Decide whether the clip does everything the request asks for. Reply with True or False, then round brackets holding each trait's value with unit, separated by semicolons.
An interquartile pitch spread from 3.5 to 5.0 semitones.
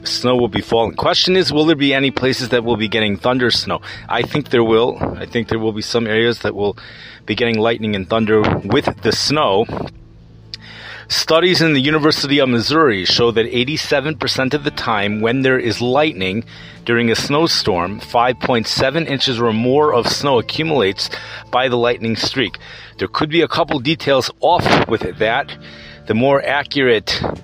True (4.2 semitones)